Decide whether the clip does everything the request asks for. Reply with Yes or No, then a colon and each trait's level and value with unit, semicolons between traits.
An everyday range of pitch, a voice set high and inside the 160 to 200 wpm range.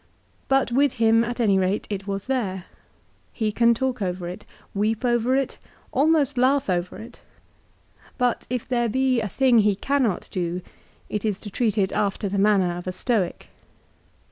Yes: average, 4.4 semitones; high, 220 Hz; average, 175 wpm